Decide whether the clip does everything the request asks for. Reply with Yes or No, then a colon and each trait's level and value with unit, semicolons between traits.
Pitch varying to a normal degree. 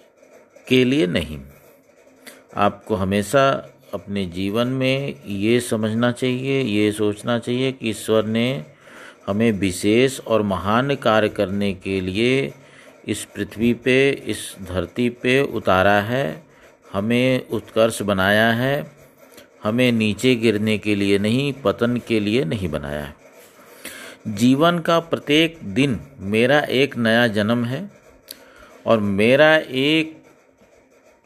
Yes: average, 4.0 semitones